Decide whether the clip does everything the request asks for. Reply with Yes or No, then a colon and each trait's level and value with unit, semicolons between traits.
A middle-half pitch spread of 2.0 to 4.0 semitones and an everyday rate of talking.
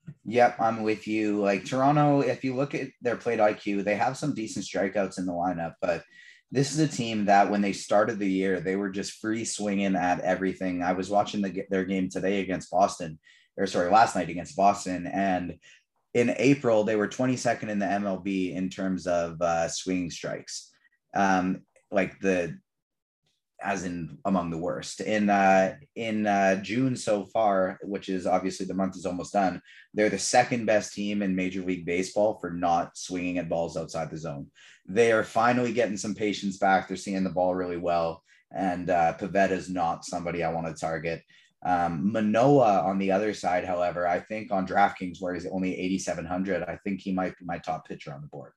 Yes: narrow, 2.6 semitones; average, 195 wpm